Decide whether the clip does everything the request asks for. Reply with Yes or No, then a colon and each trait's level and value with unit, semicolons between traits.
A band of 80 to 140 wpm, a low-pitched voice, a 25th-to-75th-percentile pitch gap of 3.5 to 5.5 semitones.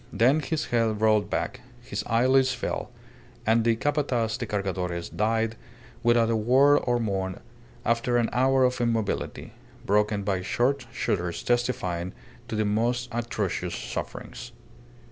No: slow, 135 wpm; low, 115 Hz; average, 2.9 semitones